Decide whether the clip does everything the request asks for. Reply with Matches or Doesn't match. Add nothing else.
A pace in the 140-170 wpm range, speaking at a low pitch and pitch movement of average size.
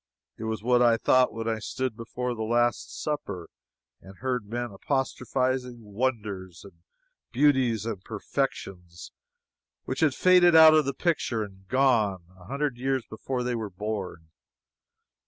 Matches